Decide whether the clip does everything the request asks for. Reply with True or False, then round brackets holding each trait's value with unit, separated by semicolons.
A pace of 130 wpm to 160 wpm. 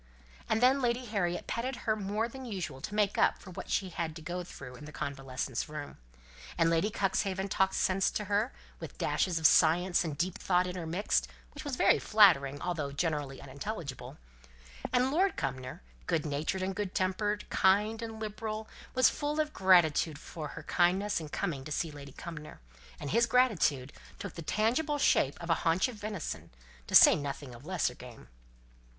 False (180 wpm)